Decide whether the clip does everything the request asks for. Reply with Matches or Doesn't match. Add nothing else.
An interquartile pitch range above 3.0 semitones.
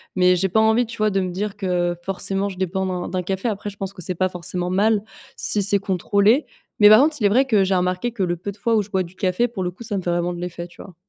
Doesn't match